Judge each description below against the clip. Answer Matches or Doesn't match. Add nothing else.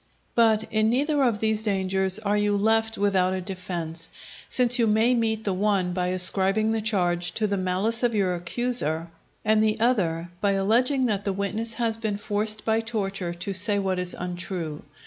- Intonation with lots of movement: Doesn't match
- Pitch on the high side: Matches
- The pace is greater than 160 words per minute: Matches